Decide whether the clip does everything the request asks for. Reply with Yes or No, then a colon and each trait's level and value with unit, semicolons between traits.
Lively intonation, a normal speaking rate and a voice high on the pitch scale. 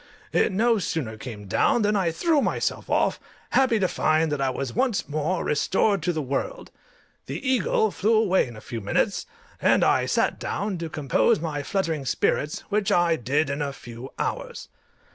No: wide, 6.9 semitones; average, 180 wpm; medium, 160 Hz